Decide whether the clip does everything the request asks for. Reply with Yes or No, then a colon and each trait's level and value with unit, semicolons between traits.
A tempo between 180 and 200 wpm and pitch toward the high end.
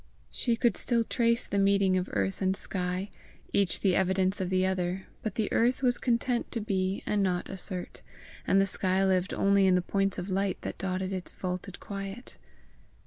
Yes: average, 190 wpm; high, 195 Hz